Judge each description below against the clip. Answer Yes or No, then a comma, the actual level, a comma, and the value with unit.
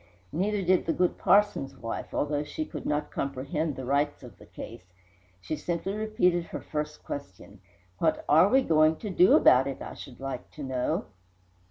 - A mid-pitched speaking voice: Yes, medium, 150 Hz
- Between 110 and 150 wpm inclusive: No, average, 180 wpm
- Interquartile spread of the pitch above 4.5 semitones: Yes, average, 4.9 semitones